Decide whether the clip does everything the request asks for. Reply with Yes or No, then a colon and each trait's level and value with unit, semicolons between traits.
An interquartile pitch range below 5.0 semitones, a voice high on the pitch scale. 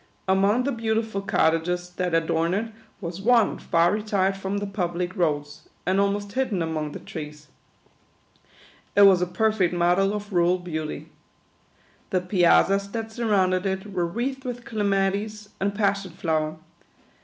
Yes: average, 3.1 semitones; high, 195 Hz